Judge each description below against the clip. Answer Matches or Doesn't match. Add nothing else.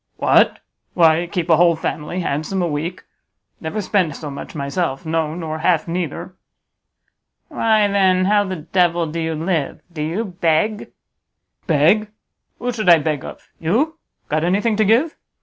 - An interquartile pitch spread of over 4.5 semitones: Doesn't match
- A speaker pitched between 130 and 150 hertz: Doesn't match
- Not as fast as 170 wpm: Matches